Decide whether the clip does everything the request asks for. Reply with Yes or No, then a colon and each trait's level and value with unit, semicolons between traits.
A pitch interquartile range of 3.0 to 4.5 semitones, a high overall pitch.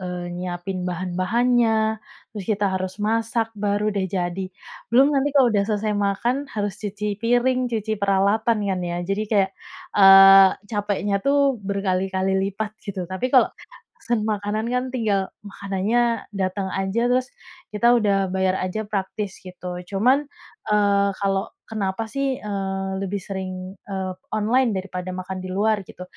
No: narrow, 2.6 semitones; high, 200 Hz